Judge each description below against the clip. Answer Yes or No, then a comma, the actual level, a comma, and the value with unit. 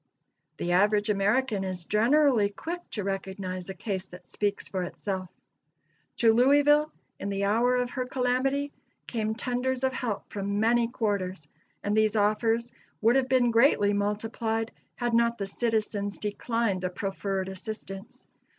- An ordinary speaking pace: Yes, average, 145 wpm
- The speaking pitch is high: Yes, high, 215 Hz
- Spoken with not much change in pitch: No, average, 3.6 semitones